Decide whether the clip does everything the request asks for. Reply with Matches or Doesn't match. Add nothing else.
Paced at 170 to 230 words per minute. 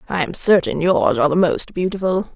Matches